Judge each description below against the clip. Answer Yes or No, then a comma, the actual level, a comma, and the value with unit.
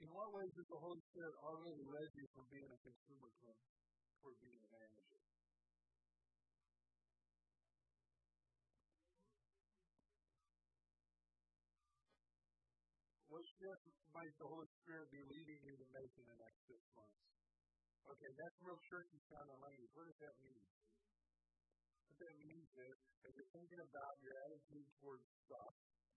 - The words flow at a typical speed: No, slow, 130 wpm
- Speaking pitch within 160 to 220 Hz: No, low, 130 Hz